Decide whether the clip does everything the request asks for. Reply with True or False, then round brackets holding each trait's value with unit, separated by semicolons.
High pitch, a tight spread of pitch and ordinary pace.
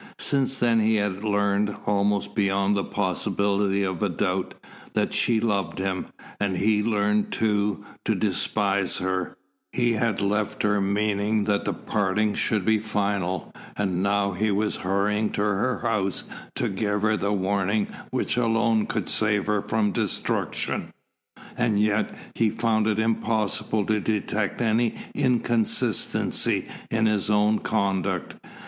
False (105 Hz; 1.7 semitones; 145 wpm)